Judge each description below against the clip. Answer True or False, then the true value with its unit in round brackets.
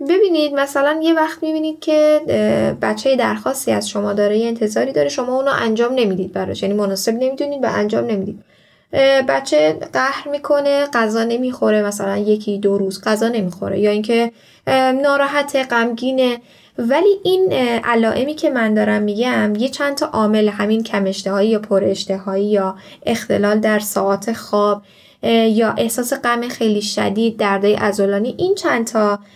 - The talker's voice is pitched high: True (230 Hz)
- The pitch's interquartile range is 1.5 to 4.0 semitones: False (4.7 semitones)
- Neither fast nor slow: True (145 wpm)